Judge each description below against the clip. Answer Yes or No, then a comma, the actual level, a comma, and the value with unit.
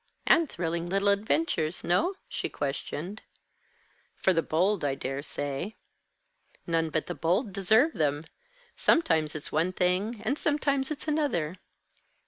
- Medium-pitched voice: Yes, medium, 180 Hz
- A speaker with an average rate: No, slow, 130 wpm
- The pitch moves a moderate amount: No, wide, 6.1 semitones